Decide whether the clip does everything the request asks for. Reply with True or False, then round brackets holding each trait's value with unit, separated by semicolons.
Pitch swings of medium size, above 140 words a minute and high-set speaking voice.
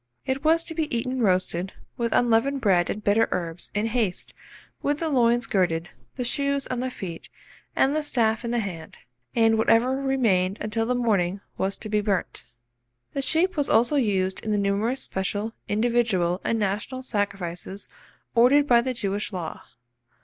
True (4.6 semitones; 170 wpm; 225 Hz)